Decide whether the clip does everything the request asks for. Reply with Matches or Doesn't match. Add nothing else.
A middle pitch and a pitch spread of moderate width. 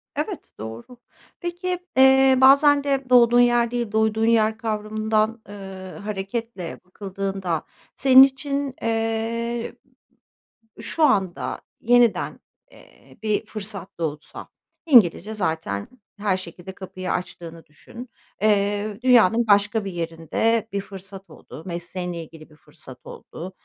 Doesn't match